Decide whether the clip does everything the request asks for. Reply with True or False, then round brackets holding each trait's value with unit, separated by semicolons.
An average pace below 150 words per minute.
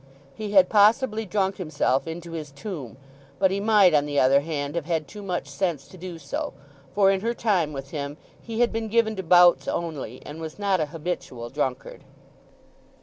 False (195 wpm)